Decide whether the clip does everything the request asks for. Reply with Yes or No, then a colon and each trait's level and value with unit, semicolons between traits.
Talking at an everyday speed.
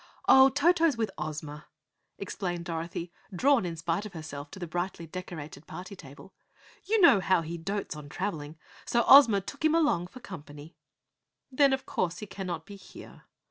Yes: average, 170 wpm